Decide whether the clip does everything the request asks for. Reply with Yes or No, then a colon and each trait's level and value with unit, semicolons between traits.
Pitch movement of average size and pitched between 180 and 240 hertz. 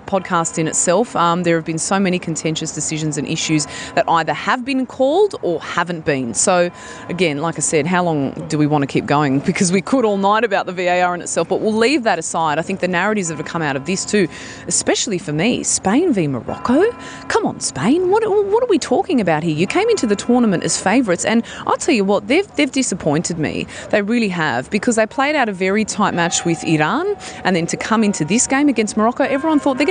No: wide, 7.1 semitones; high, 190 Hz